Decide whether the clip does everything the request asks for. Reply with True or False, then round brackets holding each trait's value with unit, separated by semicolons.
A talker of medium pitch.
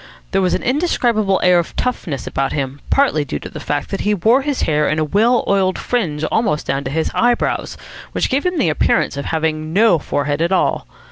True (175 Hz)